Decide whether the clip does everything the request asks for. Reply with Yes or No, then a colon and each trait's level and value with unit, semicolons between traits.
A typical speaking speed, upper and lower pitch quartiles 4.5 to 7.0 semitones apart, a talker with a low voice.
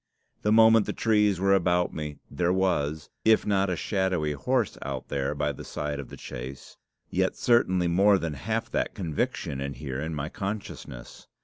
Yes: average, 180 wpm; average, 5.3 semitones; very low, 85 Hz